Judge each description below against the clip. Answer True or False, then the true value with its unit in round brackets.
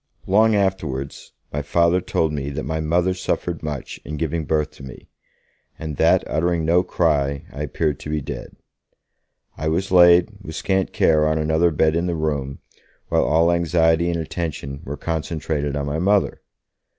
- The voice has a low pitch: True (80 Hz)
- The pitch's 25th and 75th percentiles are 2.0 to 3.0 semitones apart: True (2.5 semitones)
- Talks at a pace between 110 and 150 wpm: False (170 wpm)